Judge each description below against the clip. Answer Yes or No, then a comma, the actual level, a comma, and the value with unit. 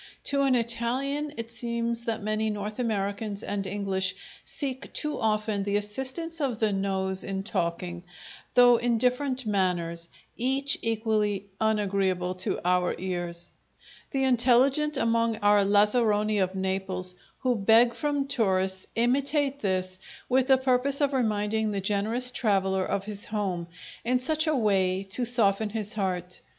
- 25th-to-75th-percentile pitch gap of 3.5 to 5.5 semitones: Yes, average, 4.3 semitones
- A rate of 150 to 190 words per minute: No, average, 140 wpm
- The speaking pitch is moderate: No, high, 215 Hz